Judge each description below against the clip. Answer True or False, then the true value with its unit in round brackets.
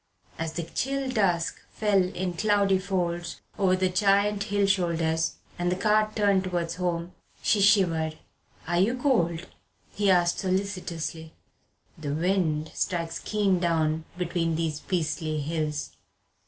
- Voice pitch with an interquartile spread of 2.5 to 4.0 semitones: True (3.2 semitones)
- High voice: False (180 Hz)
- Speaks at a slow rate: True (130 wpm)